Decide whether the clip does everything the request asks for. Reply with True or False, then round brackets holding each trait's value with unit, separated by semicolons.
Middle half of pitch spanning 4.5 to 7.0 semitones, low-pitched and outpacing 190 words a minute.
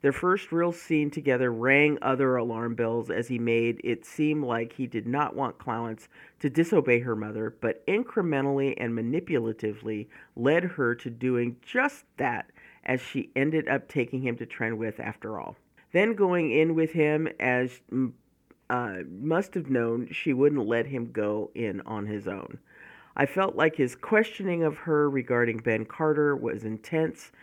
False (5.0 semitones; 130 Hz; 165 wpm)